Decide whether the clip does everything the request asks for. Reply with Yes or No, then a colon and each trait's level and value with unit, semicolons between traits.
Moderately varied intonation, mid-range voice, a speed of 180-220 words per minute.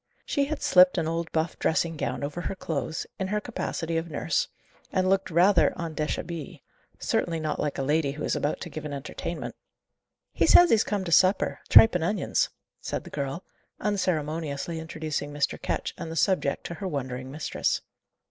Yes: average, 3.8 semitones; medium, 165 Hz; average, 185 wpm